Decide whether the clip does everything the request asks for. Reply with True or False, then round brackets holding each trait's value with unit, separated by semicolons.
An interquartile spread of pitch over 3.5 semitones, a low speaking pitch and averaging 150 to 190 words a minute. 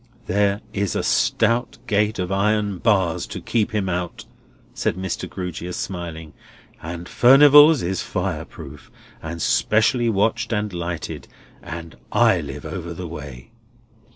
False (4.2 semitones; 95 Hz; 135 wpm)